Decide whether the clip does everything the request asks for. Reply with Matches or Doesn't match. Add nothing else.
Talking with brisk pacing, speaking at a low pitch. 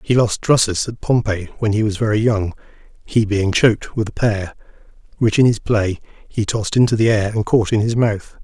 Matches